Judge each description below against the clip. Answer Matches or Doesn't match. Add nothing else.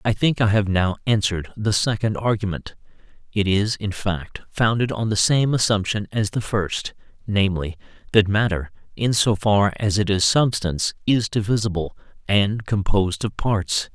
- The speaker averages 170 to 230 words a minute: Doesn't match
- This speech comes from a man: Matches